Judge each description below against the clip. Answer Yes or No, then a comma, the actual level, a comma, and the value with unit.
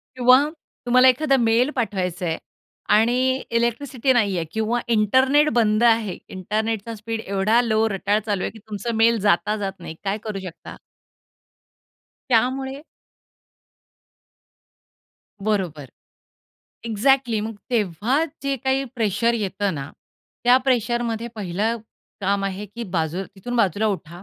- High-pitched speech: Yes, high, 220 Hz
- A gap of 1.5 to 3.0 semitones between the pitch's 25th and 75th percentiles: No, average, 3.5 semitones